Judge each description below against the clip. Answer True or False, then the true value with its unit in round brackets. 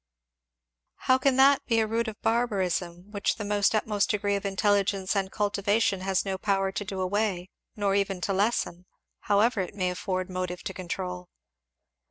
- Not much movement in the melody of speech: True (2.2 semitones)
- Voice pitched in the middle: False (200 Hz)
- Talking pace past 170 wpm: False (165 wpm)